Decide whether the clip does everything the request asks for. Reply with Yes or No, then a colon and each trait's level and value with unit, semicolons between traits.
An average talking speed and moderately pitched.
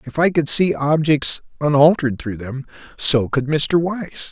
Yes: average, 165 wpm; medium, 145 Hz